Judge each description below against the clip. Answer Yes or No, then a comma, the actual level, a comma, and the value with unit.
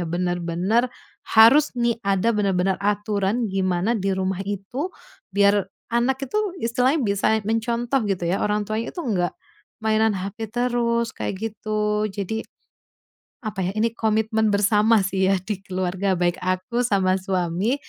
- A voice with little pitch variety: No, average, 3.3 semitones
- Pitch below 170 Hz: No, high, 205 Hz